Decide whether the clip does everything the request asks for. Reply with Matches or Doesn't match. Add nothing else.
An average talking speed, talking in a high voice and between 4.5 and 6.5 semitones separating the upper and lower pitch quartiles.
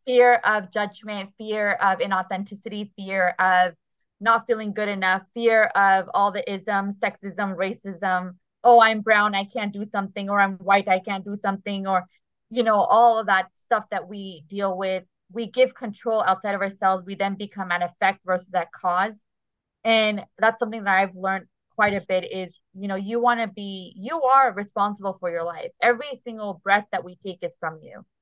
Doesn't match